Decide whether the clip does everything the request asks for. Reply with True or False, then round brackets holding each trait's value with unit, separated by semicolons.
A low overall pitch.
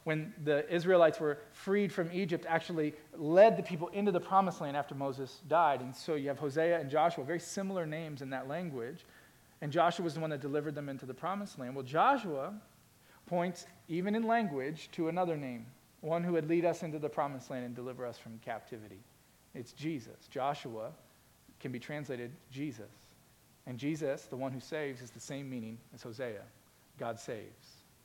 False (150 Hz)